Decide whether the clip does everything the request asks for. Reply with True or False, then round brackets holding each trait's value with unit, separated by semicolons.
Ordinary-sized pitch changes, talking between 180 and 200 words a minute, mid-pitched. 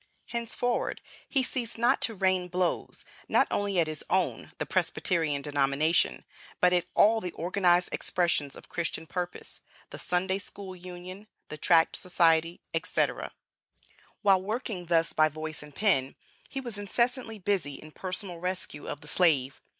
False (4.0 semitones; 150 wpm; 180 Hz)